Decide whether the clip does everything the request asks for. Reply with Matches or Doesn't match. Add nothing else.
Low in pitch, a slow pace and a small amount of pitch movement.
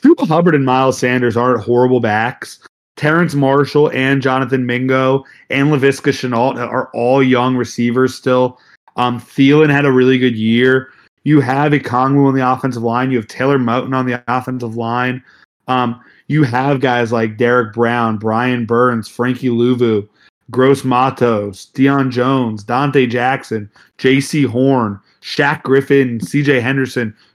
Doesn't match